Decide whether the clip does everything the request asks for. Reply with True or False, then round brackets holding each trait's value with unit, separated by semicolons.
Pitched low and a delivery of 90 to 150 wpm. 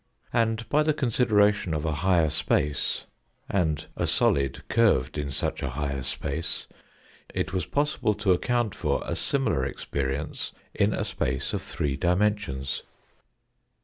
True (85 Hz; 140 wpm)